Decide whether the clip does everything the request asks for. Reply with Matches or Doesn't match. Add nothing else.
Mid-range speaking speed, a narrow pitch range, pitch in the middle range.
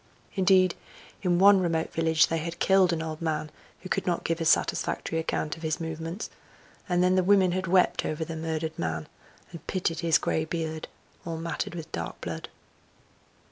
Matches